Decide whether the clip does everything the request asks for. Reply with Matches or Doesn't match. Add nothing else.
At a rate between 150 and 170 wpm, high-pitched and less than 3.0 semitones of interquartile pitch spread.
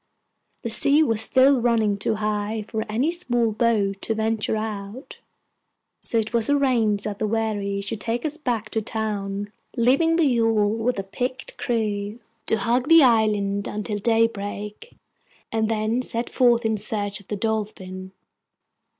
Matches